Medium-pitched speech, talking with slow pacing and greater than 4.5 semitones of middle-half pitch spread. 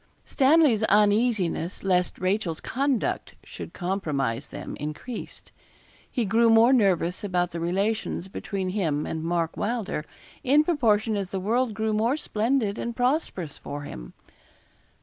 No: high, 205 Hz; slow, 130 wpm; average, 5.0 semitones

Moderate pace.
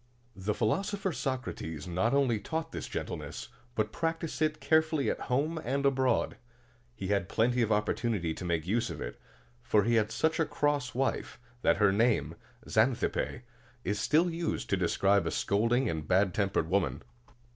Yes: average, 165 wpm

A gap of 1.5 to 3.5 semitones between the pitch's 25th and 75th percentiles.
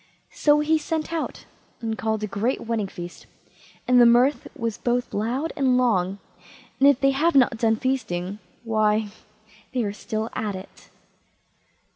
No: average, 4.1 semitones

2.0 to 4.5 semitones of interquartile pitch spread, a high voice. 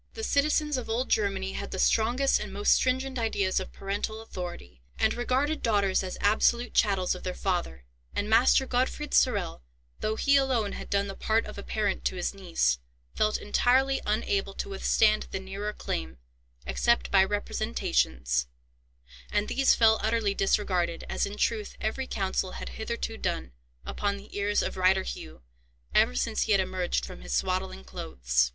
Yes: average, 3.9 semitones; high, 205 Hz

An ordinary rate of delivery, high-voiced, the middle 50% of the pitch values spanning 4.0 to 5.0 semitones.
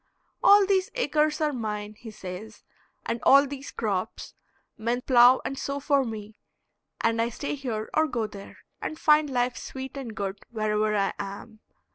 Yes: average, 165 wpm; high, 235 Hz; average, 4.7 semitones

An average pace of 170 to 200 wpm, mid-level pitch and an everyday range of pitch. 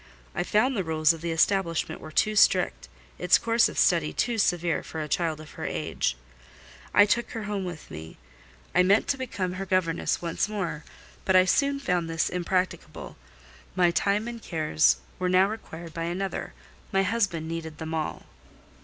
Yes: average, 175 wpm; medium, 180 Hz; average, 3.8 semitones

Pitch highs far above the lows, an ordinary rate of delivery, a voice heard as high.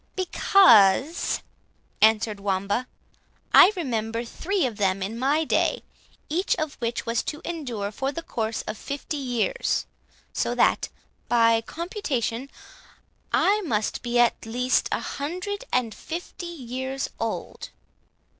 No: wide, 6.1 semitones; slow, 125 wpm; very high, 250 Hz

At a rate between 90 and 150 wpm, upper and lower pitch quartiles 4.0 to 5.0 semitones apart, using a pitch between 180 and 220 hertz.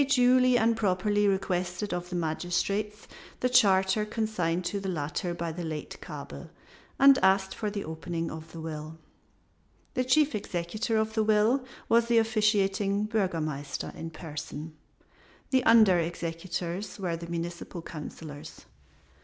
Yes: average, 140 wpm; average, 4.5 semitones; high, 190 Hz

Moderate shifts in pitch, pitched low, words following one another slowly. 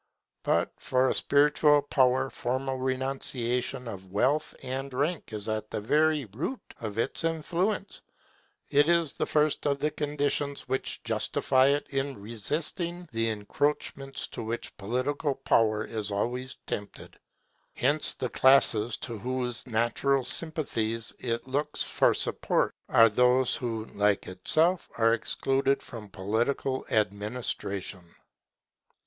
Yes: average, 4.2 semitones; low, 130 Hz; slow, 125 wpm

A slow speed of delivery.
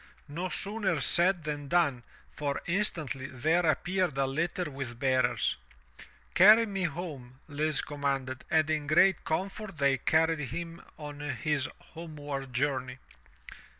Yes: slow, 130 wpm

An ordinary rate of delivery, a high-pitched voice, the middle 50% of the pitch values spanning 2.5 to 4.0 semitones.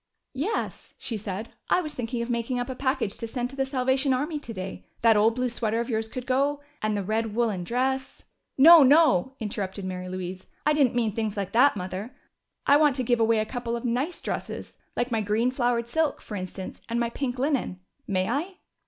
No: fast, 215 wpm; high, 235 Hz; average, 3.6 semitones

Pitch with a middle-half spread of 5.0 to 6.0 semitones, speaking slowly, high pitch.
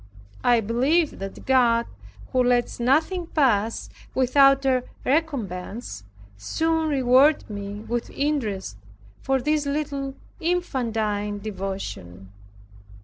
Yes: wide, 5.5 semitones; slow, 95 wpm; very high, 250 Hz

